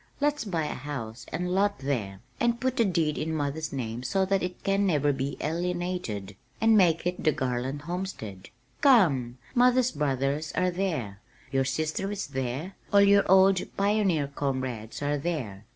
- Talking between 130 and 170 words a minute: Yes, average, 165 wpm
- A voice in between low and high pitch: Yes, medium, 155 Hz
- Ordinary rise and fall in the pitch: No, wide, 6.4 semitones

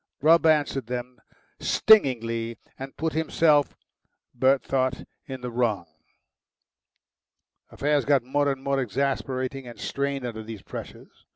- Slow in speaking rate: Yes, slow, 120 wpm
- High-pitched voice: No, low, 135 Hz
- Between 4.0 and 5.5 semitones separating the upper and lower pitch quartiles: No, narrow, 2.6 semitones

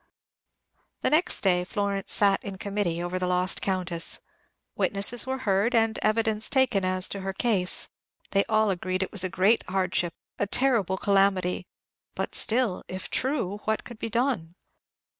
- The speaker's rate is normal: Yes, average, 160 wpm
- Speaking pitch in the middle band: No, high, 200 Hz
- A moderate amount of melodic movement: Yes, average, 3.2 semitones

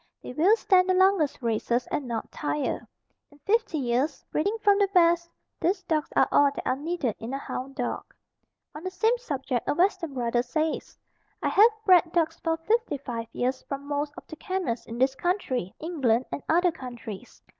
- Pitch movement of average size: No, wide, 5.9 semitones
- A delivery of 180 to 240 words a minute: Yes, average, 185 wpm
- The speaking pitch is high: Yes, very high, 300 Hz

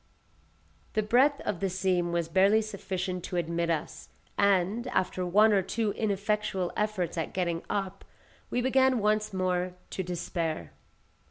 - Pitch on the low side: No, high, 190 Hz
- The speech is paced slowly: No, average, 145 wpm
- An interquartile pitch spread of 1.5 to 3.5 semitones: Yes, average, 3.1 semitones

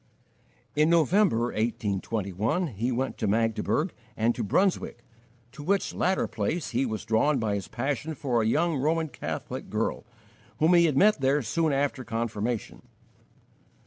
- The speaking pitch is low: Yes, low, 130 Hz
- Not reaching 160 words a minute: Yes, average, 145 wpm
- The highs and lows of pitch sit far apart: Yes, wide, 6.0 semitones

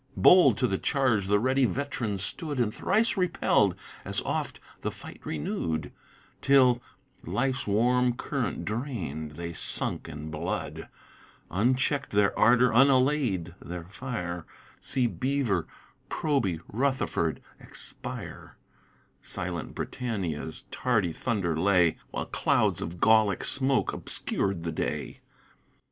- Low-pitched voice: Yes, low, 110 Hz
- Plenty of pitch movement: Yes, wide, 6.8 semitones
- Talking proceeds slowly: Yes, slow, 115 wpm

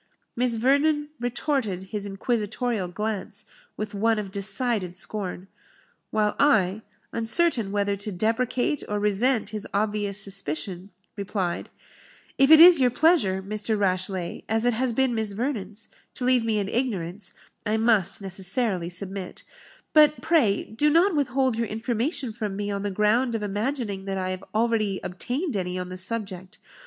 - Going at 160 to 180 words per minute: No, average, 150 wpm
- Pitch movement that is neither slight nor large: Yes, average, 4.0 semitones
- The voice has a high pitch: Yes, high, 215 Hz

